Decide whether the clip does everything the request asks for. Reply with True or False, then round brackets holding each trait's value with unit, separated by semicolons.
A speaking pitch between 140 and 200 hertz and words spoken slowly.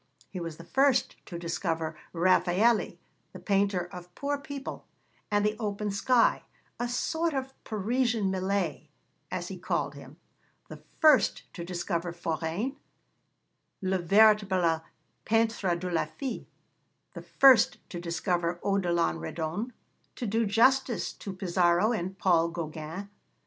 True (190 Hz; 130 wpm)